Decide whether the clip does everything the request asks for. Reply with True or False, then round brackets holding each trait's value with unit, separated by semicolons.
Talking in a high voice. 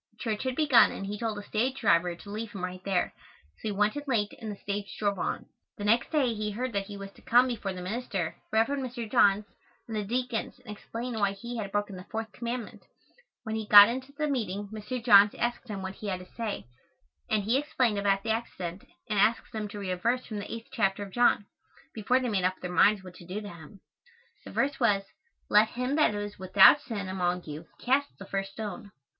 True (210 Hz)